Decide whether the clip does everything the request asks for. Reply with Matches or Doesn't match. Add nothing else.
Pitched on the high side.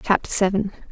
Matches